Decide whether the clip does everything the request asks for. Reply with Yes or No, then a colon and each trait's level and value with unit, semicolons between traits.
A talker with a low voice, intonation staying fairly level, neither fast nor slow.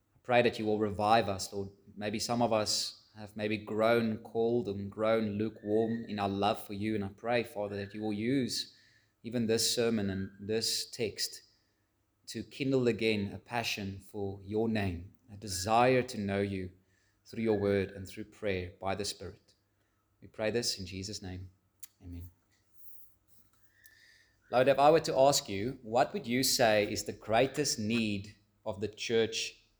Yes: low, 105 Hz; narrow, 2.2 semitones; average, 170 wpm